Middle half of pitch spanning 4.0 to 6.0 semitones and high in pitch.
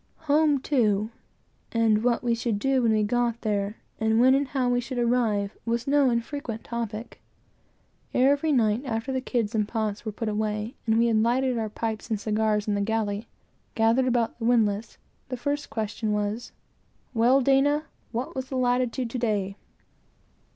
No: average, 2.9 semitones; high, 230 Hz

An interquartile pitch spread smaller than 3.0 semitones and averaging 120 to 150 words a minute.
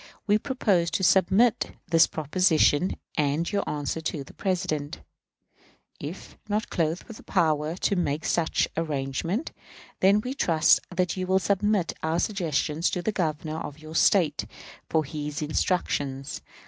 No: average, 3.8 semitones; average, 140 wpm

